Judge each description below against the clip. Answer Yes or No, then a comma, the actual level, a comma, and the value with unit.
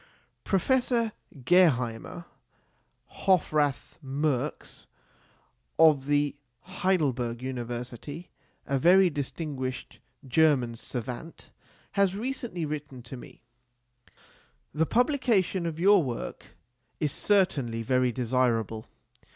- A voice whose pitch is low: No, medium, 145 Hz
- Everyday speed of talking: No, slow, 85 wpm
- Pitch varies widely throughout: Yes, wide, 6.3 semitones